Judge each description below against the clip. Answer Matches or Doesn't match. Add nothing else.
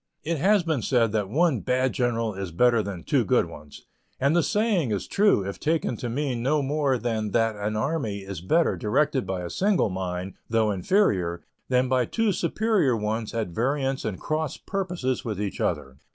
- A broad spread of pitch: Matches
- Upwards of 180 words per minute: Matches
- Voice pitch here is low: Matches